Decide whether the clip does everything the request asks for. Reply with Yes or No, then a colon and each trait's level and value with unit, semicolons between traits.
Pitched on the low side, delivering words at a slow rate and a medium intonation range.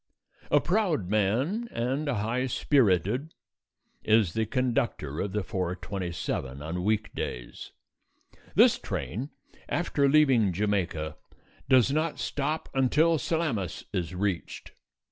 No: low, 110 Hz; slow, 105 wpm; wide, 7.3 semitones